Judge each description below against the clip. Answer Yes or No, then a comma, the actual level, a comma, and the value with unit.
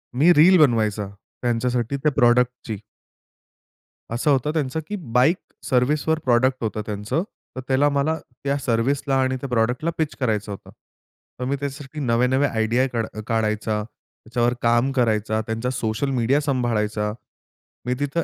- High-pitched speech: No, low, 125 Hz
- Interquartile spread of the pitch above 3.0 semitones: Yes, average, 3.6 semitones